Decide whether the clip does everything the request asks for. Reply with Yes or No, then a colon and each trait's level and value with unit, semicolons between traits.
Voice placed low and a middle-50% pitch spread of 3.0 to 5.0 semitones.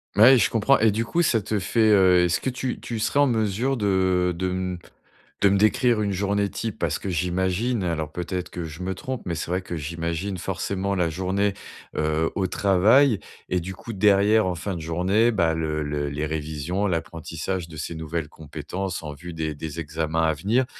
Yes: very low, 90 Hz; average, 3.9 semitones